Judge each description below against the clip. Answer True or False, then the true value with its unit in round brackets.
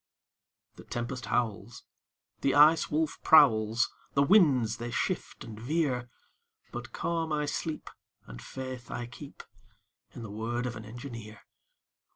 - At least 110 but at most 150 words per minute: True (135 wpm)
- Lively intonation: False (4.3 semitones)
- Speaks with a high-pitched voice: False (120 Hz)